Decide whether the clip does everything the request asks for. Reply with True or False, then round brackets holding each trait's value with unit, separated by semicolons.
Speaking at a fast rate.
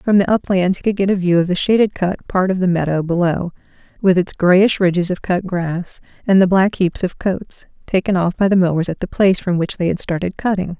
True (245 wpm)